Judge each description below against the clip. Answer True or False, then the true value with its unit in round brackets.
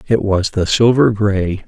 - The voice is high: False (105 Hz)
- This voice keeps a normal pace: True (180 wpm)